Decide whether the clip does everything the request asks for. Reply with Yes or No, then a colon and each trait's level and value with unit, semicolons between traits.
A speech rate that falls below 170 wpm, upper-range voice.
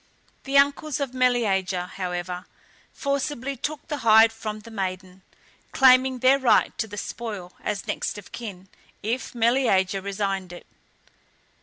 Yes: slow, 135 wpm; high, 225 Hz